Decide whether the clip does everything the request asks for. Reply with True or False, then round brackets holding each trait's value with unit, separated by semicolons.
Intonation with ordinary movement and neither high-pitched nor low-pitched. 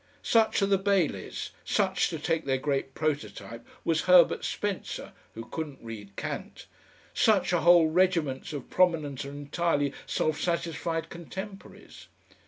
True (4.5 semitones; 160 Hz)